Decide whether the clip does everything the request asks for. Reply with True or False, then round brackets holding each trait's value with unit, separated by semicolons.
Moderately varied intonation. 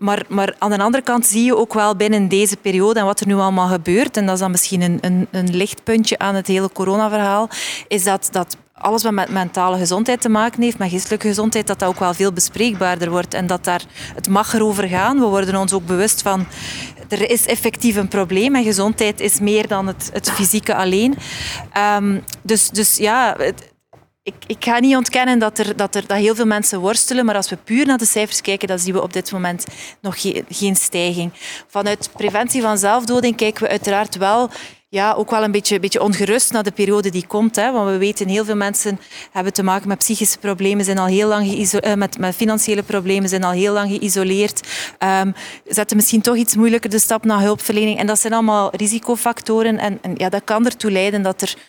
False (2.1 semitones)